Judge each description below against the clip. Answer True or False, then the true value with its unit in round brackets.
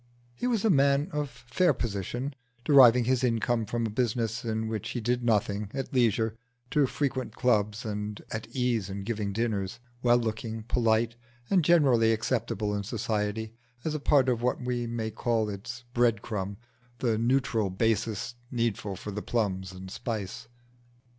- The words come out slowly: False (160 wpm)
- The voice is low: True (115 Hz)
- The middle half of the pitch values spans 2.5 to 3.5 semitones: True (2.8 semitones)